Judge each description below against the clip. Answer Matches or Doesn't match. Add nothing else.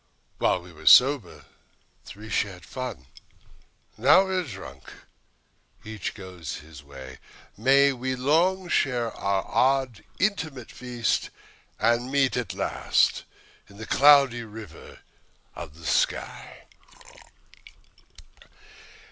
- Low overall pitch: Matches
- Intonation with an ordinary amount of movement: Doesn't match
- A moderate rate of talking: Doesn't match